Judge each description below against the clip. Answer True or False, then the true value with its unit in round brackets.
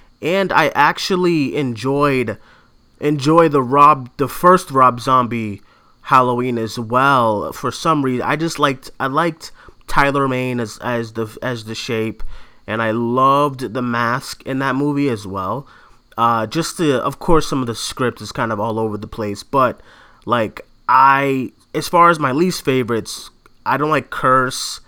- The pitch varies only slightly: False (3.7 semitones)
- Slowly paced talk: False (165 wpm)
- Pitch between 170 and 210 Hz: False (130 Hz)